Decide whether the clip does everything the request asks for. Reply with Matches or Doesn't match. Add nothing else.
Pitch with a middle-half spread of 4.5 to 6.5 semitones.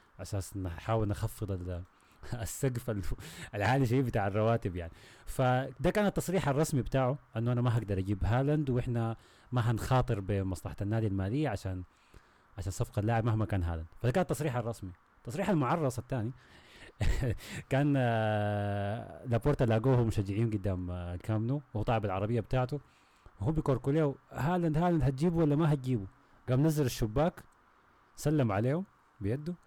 Matches